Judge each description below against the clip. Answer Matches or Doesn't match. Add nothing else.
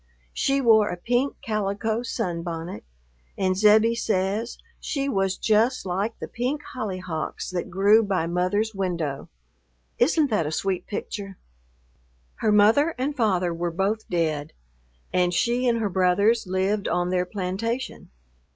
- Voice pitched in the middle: Doesn't match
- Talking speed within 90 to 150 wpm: Matches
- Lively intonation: Doesn't match